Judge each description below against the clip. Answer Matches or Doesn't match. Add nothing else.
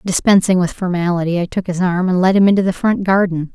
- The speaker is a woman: Matches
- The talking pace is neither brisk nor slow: Doesn't match